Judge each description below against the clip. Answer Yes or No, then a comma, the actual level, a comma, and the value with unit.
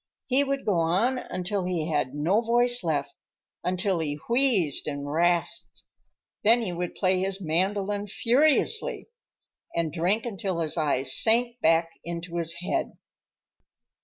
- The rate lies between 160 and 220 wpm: No, slow, 135 wpm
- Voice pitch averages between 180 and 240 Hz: Yes, medium, 185 Hz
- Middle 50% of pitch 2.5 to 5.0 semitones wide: No, wide, 5.6 semitones